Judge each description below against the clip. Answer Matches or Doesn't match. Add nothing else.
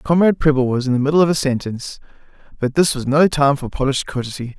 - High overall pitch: Doesn't match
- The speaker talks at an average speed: Doesn't match